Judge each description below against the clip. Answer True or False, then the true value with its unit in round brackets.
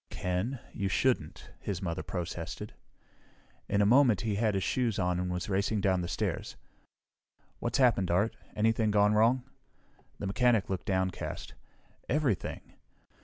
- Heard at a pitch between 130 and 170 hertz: False (100 Hz)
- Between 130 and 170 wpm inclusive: True (140 wpm)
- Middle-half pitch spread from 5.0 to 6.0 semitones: False (3.7 semitones)